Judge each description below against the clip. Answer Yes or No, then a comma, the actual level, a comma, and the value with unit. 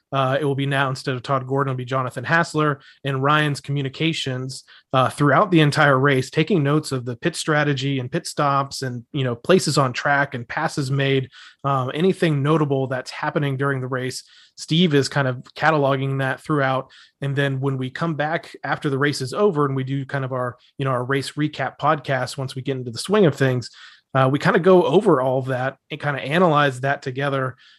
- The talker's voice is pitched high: No, medium, 140 Hz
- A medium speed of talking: No, fast, 215 wpm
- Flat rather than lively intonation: Yes, narrow, 2.3 semitones